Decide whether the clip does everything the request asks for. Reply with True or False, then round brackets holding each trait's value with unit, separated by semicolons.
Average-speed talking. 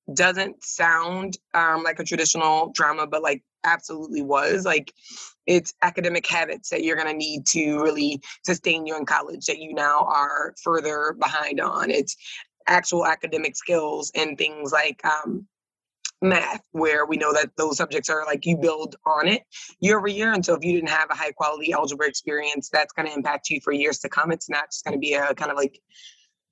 True (195 wpm)